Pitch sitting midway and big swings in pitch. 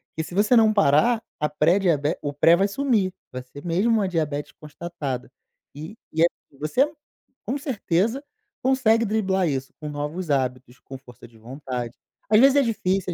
Yes: medium, 170 Hz; wide, 7.1 semitones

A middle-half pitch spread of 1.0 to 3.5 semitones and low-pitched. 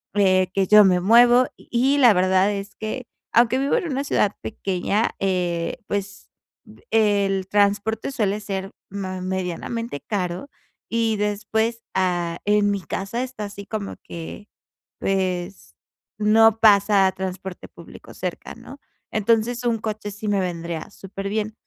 No: average, 2.9 semitones; high, 205 Hz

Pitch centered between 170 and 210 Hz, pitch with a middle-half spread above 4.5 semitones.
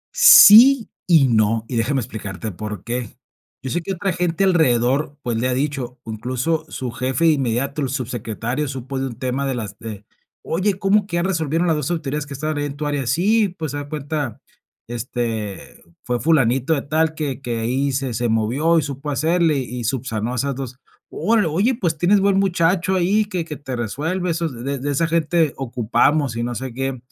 No: medium, 140 Hz; average, 5.2 semitones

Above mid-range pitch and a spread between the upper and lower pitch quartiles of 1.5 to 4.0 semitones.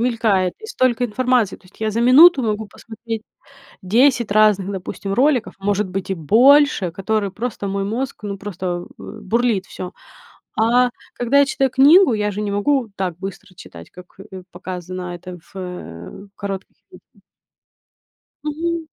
No: high, 210 Hz; average, 4.7 semitones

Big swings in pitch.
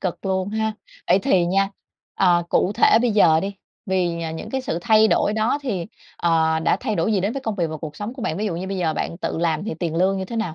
No: average, 4.2 semitones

